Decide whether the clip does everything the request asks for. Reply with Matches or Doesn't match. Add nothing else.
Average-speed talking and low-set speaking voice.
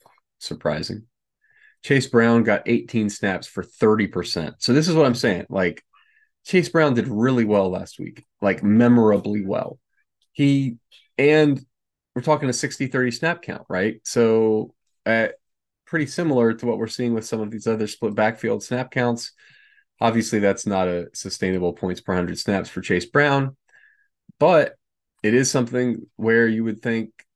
Matches